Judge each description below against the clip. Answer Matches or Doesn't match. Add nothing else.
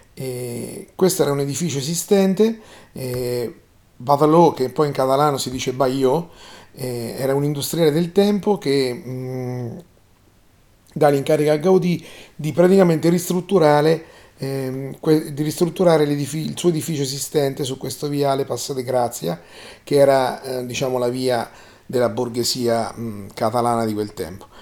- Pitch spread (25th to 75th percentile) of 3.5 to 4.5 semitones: Matches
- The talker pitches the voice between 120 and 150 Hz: Matches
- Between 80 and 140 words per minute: Matches